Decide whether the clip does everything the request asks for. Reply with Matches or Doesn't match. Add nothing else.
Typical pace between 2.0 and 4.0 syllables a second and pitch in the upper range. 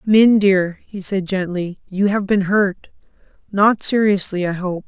Matches